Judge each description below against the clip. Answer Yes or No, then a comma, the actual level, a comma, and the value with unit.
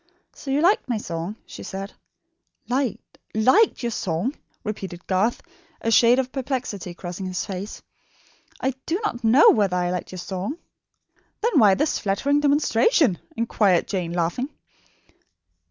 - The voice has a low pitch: No, high, 220 Hz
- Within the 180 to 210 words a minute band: No, average, 140 wpm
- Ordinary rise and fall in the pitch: No, wide, 6.3 semitones